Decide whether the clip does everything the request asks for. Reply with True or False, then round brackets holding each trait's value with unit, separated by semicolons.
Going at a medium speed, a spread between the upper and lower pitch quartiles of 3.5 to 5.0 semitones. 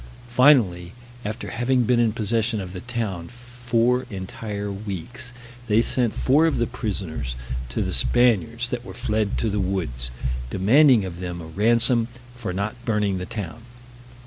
True (155 wpm; 4.2 semitones)